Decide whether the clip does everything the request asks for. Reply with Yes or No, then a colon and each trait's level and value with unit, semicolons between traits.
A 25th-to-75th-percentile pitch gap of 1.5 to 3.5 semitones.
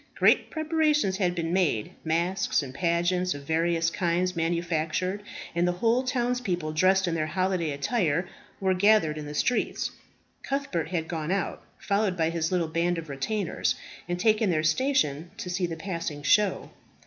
Yes: average, 3.2 semitones